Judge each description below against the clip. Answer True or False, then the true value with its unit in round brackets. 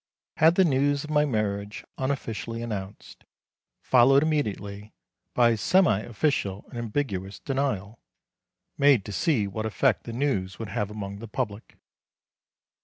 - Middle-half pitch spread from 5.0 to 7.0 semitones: True (5.4 semitones)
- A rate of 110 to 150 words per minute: True (135 wpm)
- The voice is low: True (115 Hz)